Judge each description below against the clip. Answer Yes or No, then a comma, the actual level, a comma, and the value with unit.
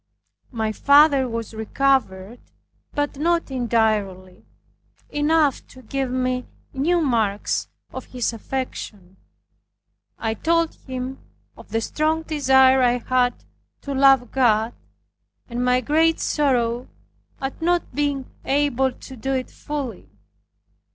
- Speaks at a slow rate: Yes, slow, 115 wpm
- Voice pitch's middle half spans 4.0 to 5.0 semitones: No, average, 3.6 semitones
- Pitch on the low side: No, very high, 260 Hz